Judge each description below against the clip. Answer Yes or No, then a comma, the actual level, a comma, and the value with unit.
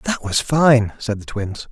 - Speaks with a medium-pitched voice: No, low, 120 Hz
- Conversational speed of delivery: No, fast, 210 wpm